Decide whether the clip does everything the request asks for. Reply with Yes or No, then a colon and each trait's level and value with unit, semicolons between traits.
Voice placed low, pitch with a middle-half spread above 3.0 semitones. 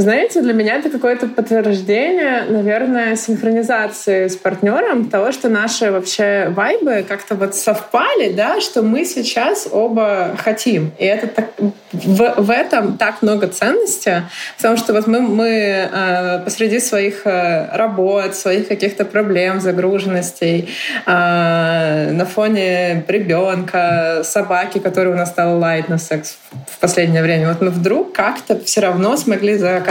No: high, 205 Hz; average, 3.6 semitones